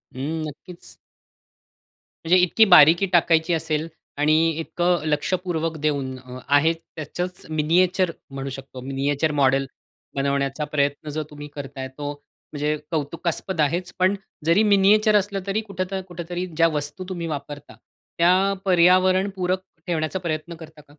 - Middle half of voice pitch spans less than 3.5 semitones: No, average, 3.8 semitones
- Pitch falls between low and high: Yes, medium, 160 Hz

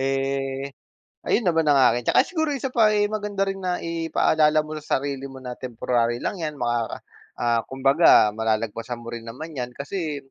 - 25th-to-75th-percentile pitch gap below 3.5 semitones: No, average, 5.3 semitones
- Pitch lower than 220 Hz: Yes, low, 135 Hz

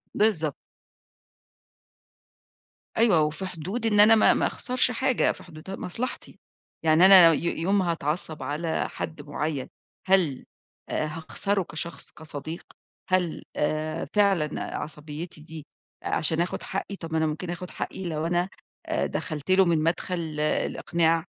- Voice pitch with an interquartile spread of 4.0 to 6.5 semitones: No, average, 3.4 semitones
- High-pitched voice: No, medium, 165 Hz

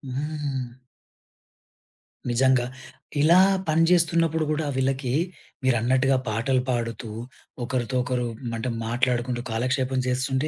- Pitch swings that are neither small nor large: Yes, average, 3.1 semitones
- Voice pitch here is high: No, low, 130 Hz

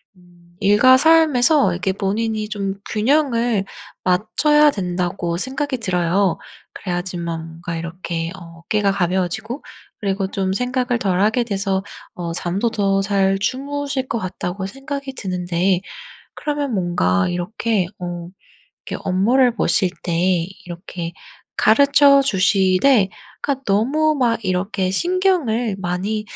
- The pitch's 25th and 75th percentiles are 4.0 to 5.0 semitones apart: No, wide, 5.6 semitones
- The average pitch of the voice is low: No, high, 195 Hz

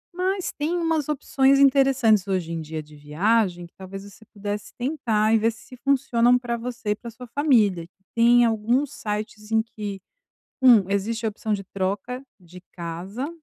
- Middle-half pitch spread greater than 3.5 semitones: Yes, average, 4.3 semitones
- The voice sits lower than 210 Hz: No, high, 220 Hz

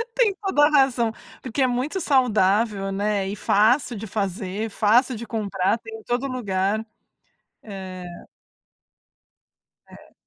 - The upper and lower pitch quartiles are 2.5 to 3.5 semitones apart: No, average, 4.3 semitones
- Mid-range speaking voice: No, high, 220 Hz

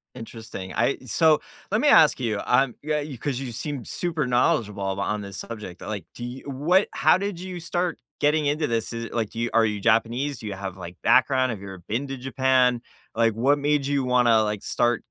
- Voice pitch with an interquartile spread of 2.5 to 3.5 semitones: No, average, 4.7 semitones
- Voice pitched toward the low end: Yes, low, 125 Hz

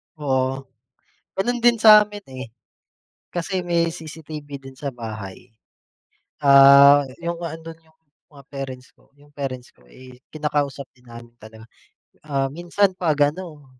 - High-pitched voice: No, medium, 145 Hz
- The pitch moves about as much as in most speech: Yes, average, 4.2 semitones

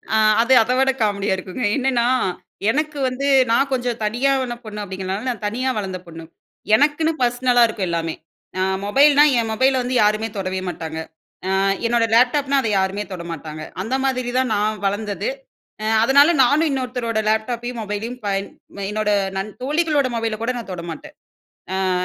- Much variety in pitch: No, average, 4.2 semitones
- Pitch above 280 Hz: No, high, 230 Hz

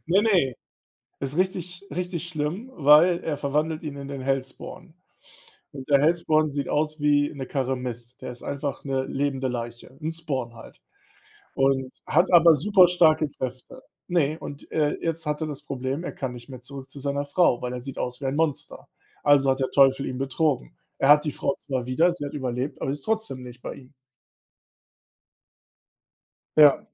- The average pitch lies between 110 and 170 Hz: Yes, medium, 140 Hz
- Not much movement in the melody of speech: No, average, 3.1 semitones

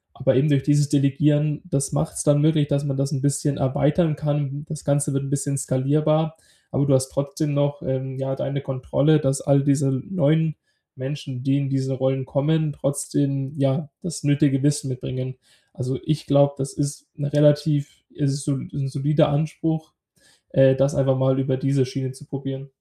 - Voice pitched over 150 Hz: No, medium, 140 Hz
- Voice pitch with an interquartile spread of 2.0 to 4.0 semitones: No, narrow, 1.5 semitones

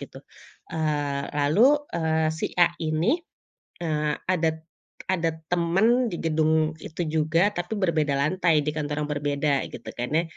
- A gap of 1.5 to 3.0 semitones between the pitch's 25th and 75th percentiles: Yes, narrow, 2.5 semitones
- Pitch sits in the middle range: Yes, medium, 160 Hz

